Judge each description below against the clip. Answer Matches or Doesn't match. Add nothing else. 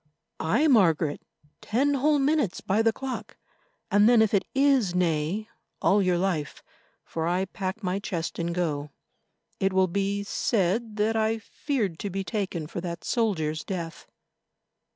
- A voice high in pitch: Matches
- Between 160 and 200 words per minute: Doesn't match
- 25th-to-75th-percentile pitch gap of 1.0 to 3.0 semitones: Doesn't match